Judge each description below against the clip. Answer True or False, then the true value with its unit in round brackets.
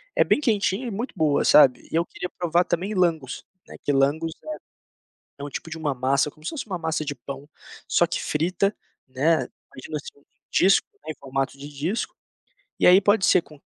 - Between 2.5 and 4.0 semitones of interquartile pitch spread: False (4.5 semitones)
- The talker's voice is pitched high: False (160 Hz)